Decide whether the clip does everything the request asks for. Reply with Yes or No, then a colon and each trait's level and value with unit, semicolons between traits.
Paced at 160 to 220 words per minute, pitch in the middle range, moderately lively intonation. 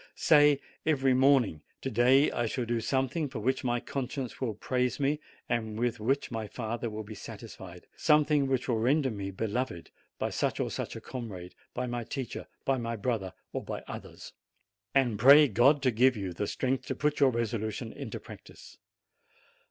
No: average, 180 wpm; low, 120 Hz; average, 3.4 semitones